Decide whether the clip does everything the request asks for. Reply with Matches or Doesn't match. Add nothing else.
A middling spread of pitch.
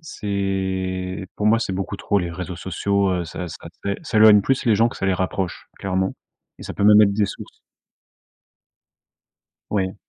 Doesn't match